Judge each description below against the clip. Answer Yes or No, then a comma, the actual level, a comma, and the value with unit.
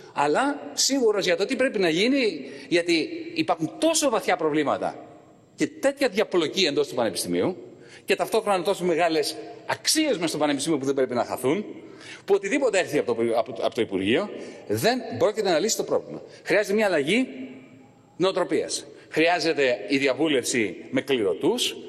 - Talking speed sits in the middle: Yes, average, 145 wpm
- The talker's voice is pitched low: No, high, 200 Hz